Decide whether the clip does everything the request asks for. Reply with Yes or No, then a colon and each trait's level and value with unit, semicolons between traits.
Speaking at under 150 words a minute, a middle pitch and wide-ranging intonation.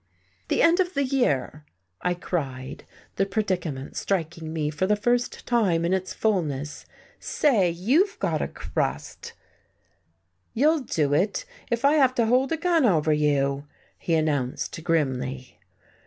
Yes: average, 140 wpm; medium, 180 Hz; wide, 8.5 semitones